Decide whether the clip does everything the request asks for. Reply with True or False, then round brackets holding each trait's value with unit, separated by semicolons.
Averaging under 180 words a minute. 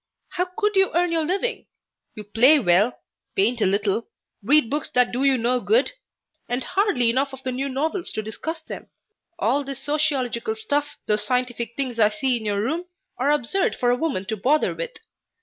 False (190 wpm)